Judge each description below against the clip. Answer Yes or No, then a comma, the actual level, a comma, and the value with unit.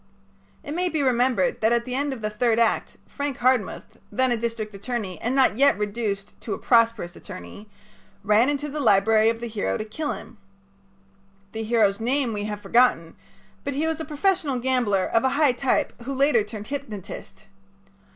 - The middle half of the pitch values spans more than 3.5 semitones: Yes, average, 4.1 semitones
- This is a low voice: No, high, 235 Hz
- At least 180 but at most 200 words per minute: Yes, average, 185 wpm